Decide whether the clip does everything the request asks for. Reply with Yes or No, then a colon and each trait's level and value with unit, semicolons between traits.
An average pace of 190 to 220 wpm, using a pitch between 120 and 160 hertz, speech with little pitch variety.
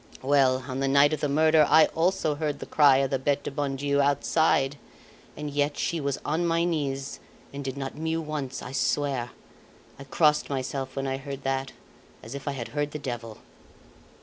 Yes: average, 200 wpm; medium, 140 Hz; narrow, 1.9 semitones